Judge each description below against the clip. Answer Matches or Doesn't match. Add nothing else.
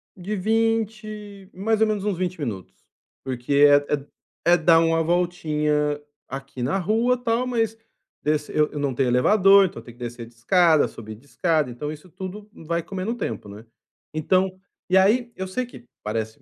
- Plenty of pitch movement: Matches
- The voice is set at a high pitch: Doesn't match